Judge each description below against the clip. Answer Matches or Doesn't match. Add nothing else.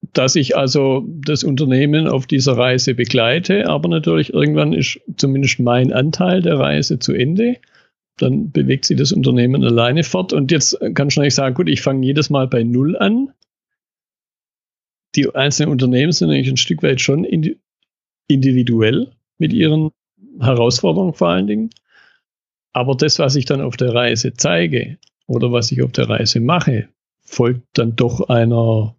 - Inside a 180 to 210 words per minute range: Doesn't match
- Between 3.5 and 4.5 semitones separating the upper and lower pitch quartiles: Matches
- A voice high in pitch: Doesn't match